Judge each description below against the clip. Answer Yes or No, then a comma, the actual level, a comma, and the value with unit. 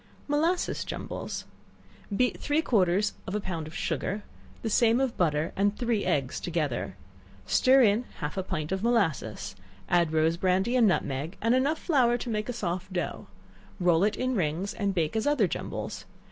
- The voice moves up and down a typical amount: No, wide, 6.0 semitones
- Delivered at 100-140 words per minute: No, average, 175 wpm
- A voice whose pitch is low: No, high, 200 Hz